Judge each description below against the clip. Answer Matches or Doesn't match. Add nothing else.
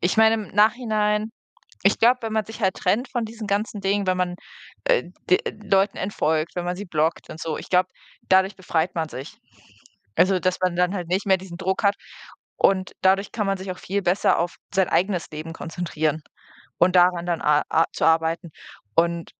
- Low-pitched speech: Doesn't match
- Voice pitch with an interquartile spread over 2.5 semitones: Matches